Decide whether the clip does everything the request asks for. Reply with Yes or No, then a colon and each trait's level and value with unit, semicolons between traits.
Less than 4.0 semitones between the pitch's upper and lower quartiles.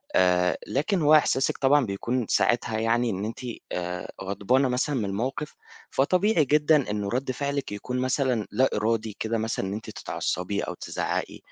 No: average, 5.0 semitones